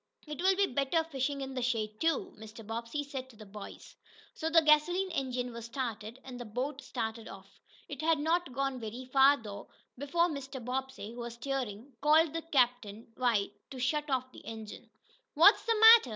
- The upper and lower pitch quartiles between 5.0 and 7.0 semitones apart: No, average, 4.5 semitones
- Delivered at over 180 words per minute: Yes, average, 190 wpm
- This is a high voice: Yes, very high, 260 Hz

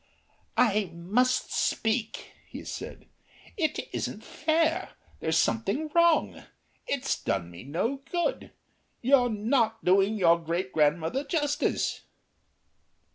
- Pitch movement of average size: No, wide, 8.8 semitones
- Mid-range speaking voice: No, high, 225 Hz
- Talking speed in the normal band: No, slow, 105 wpm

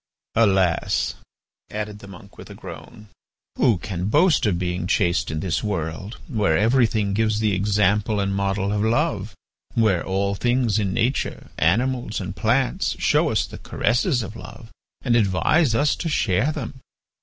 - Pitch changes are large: No, average, 3.4 semitones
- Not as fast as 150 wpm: No, average, 155 wpm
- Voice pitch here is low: Yes, low, 105 Hz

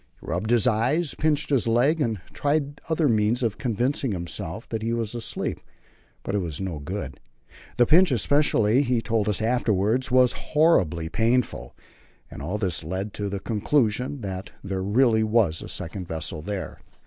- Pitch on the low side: Yes, low, 110 Hz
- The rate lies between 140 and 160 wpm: No, average, 170 wpm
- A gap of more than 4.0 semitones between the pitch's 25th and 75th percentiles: Yes, average, 4.7 semitones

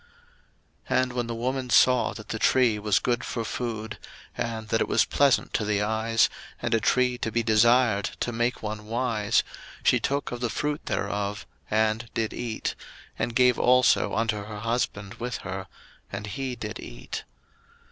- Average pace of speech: Yes, average, 175 wpm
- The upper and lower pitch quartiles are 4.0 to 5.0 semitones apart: No, narrow, 2.6 semitones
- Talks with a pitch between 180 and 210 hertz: No, low, 115 Hz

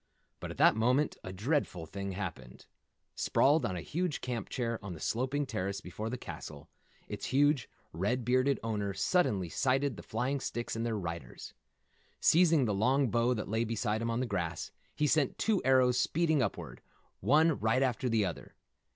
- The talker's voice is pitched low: Yes, low, 115 Hz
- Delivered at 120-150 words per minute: No, average, 175 wpm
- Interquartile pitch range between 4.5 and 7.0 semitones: Yes, average, 5.3 semitones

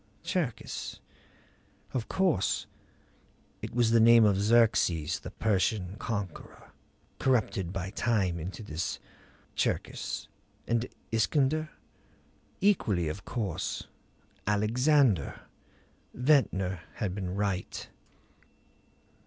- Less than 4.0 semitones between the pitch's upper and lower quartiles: No, average, 4.4 semitones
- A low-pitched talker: Yes, low, 105 Hz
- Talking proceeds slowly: Yes, slow, 85 wpm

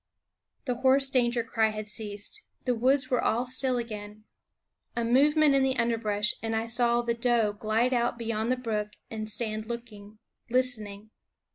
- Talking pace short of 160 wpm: No, average, 165 wpm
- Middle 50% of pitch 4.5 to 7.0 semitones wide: No, average, 2.7 semitones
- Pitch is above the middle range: Yes, high, 235 Hz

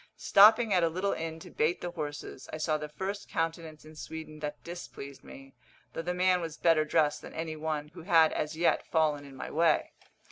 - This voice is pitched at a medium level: Yes, medium, 160 Hz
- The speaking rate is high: Yes, fast, 210 wpm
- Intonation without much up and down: Yes, narrow, 2.2 semitones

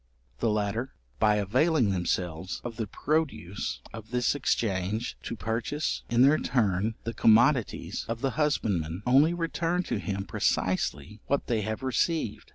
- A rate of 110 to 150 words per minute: Yes, average, 145 wpm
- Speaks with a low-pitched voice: Yes, low, 115 Hz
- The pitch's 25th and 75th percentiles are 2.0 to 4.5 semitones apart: No, average, 5.1 semitones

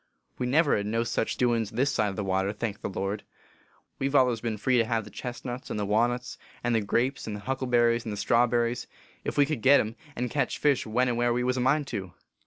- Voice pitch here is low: Yes, low, 120 Hz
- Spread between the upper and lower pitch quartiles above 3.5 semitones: No, average, 2.9 semitones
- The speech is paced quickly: Yes, fast, 250 wpm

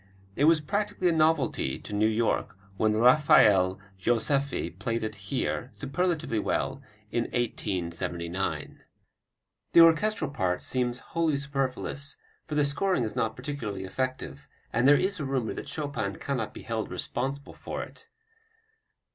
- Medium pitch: No, low, 130 Hz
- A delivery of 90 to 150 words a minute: Yes, average, 140 wpm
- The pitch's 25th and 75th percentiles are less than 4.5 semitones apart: No, wide, 5.4 semitones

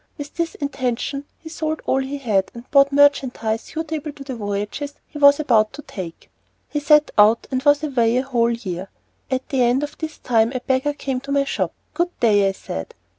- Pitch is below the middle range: No, very high, 270 Hz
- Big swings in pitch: No, average, 3.8 semitones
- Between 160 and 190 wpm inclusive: No, fast, 205 wpm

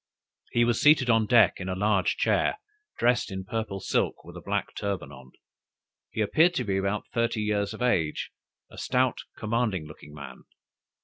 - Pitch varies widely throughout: No, average, 3.9 semitones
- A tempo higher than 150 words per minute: Yes, average, 175 wpm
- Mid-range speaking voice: No, low, 105 Hz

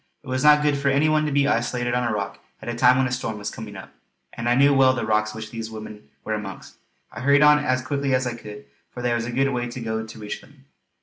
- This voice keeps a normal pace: No, fast, 285 wpm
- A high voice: No, low, 125 Hz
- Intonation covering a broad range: No, average, 3.8 semitones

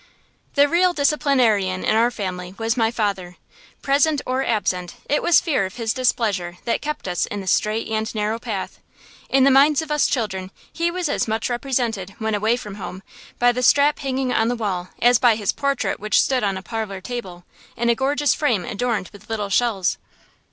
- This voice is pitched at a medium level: No, high, 230 Hz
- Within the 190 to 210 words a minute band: Yes, average, 195 wpm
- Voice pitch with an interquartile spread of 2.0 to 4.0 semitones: No, average, 5.2 semitones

